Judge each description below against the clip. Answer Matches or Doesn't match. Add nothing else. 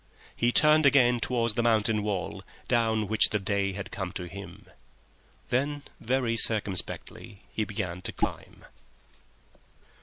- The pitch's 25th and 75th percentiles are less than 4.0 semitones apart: Matches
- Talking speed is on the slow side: Matches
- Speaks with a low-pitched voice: Matches